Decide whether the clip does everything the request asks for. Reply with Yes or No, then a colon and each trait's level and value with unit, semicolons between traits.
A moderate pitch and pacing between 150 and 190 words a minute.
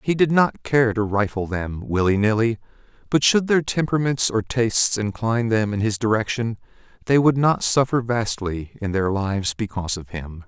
No: low, 110 Hz; average, 180 wpm